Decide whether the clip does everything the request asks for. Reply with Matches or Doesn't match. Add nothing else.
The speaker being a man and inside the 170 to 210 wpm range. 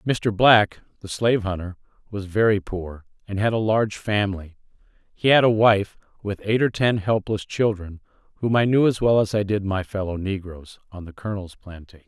Matches